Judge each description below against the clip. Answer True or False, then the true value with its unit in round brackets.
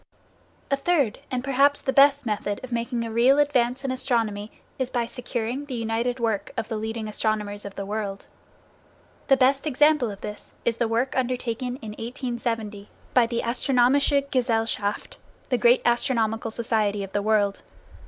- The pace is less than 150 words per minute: False (165 wpm)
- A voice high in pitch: True (235 Hz)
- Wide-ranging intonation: False (3.0 semitones)